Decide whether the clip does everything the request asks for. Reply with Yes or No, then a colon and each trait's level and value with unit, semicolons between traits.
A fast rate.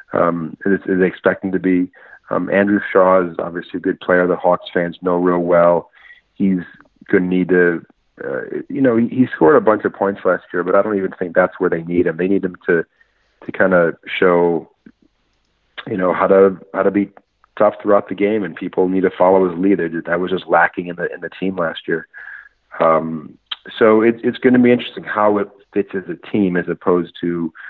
Yes: fast, 215 wpm